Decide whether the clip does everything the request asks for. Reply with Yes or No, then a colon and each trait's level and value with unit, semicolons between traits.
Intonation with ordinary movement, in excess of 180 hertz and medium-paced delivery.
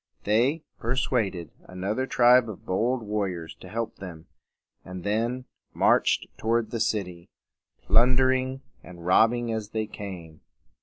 No: average, 4.8 semitones; low, 110 Hz; average, 150 wpm